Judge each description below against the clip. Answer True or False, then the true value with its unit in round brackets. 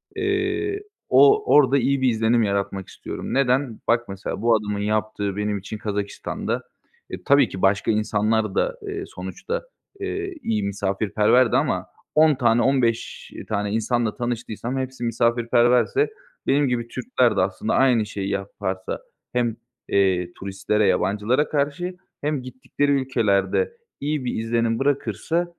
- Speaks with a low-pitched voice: True (115 Hz)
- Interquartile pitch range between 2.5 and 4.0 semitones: False (4.6 semitones)